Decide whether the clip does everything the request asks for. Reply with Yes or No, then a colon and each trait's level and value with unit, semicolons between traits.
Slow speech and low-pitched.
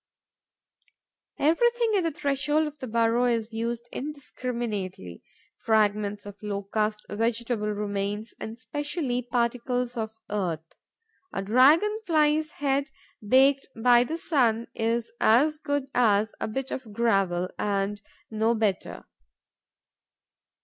No: slow, 115 wpm; high, 235 Hz